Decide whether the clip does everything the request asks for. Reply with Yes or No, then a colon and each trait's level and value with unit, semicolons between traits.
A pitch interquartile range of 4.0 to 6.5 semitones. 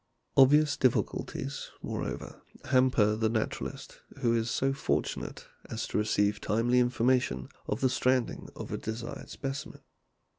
No: average, 2.9 semitones